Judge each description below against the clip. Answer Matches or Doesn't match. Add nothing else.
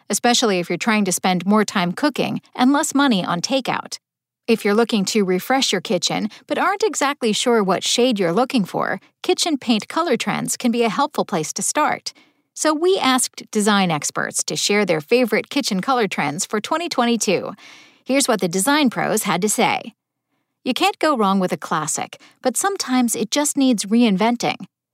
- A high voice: Matches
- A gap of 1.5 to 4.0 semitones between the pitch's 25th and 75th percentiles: Doesn't match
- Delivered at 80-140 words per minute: Doesn't match